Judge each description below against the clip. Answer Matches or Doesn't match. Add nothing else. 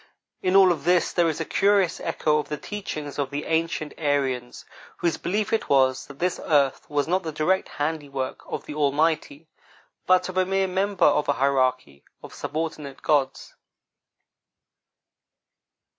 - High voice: Doesn't match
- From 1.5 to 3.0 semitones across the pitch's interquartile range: Doesn't match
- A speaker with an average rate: Matches